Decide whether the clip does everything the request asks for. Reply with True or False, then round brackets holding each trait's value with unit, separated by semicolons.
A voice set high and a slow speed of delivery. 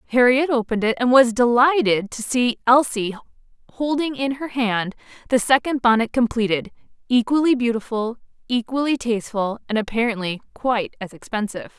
True (235 Hz; 125 wpm)